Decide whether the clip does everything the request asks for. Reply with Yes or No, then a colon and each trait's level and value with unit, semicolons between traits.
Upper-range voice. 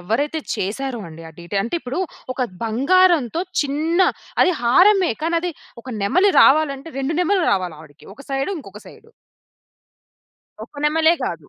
Yes: very high, 280 Hz